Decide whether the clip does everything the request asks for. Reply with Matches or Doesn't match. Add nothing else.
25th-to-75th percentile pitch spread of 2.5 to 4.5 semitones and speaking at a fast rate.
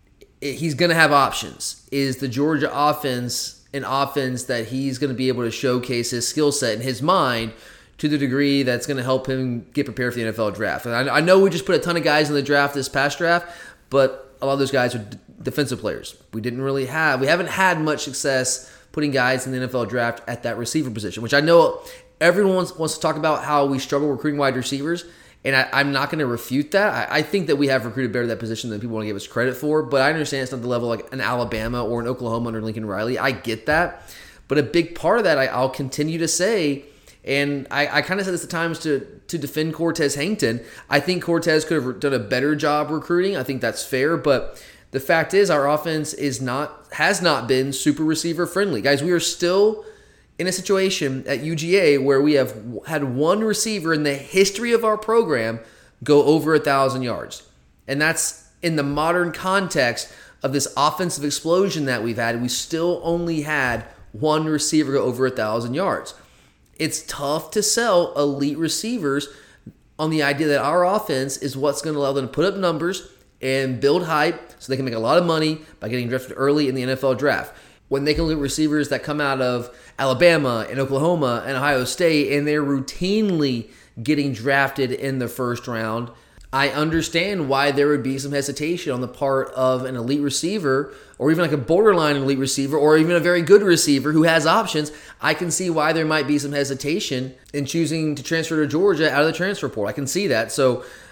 Matches